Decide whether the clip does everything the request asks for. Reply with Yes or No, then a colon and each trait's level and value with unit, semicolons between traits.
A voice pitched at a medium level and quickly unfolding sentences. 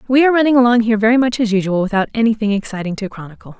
No: high, 225 Hz; fast, 235 wpm